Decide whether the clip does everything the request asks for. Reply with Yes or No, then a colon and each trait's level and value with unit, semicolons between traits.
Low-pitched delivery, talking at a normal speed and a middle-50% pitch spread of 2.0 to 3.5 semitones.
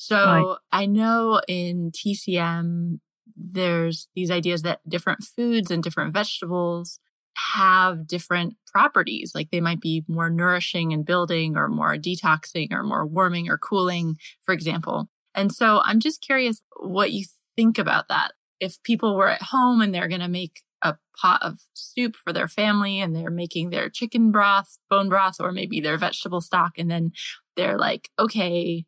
No: medium, 180 Hz; average, 165 wpm; average, 3.2 semitones